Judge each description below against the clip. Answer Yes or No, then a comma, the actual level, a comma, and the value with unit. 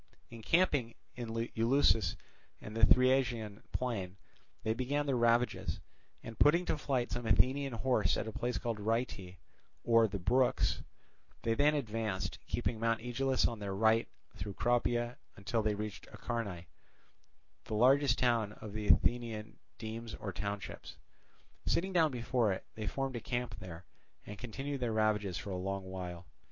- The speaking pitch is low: Yes, low, 115 Hz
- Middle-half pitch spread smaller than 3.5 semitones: Yes, average, 3.0 semitones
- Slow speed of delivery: No, average, 150 wpm